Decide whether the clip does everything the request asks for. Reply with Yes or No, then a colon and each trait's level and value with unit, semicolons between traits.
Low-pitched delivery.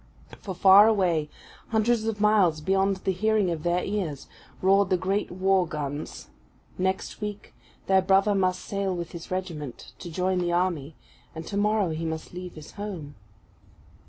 No: medium, 185 Hz